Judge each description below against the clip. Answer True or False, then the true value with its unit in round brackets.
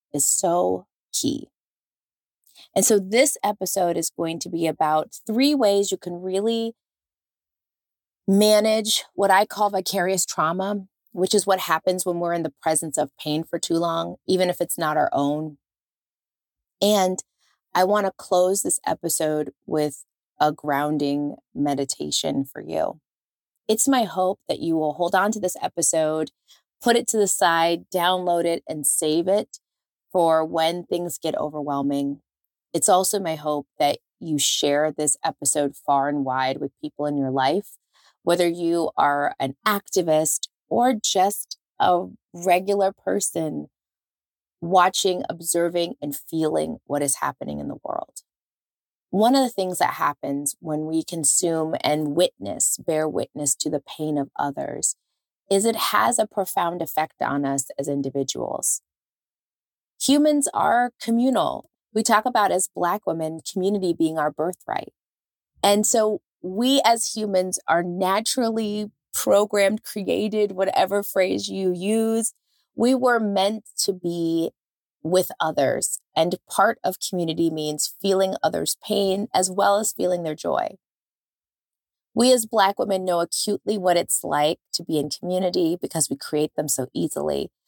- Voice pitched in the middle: True (175 Hz)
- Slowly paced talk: False (145 wpm)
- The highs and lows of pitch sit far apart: False (4.8 semitones)